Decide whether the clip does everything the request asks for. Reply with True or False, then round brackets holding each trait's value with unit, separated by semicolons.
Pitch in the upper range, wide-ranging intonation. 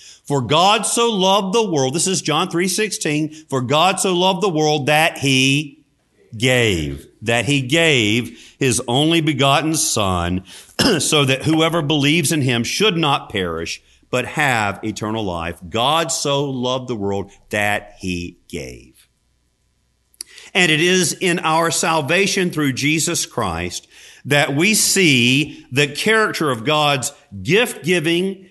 False (145 Hz; 6.1 semitones)